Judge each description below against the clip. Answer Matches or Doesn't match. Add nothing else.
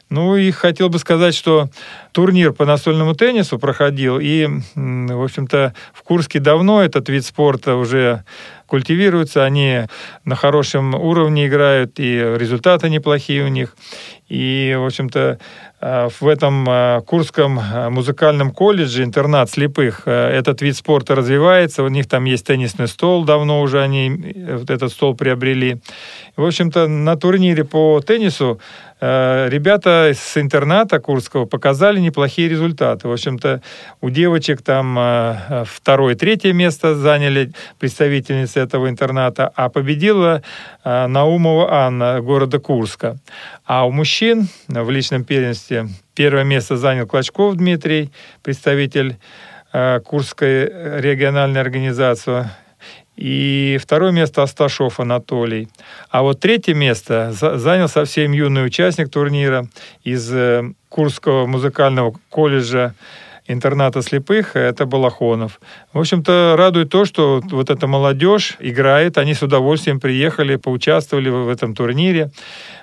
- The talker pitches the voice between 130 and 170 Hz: Matches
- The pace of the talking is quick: Doesn't match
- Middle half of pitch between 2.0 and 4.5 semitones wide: Matches